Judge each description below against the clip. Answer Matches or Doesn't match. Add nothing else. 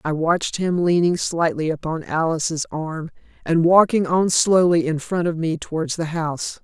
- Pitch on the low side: Doesn't match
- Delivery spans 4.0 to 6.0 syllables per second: Matches